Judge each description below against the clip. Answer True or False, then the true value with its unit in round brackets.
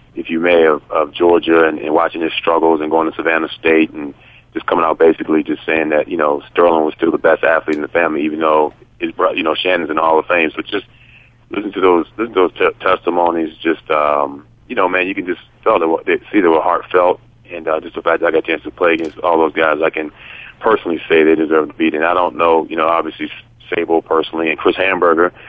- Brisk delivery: True (255 wpm)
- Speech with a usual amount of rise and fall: False (1.6 semitones)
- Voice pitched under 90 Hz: True (80 Hz)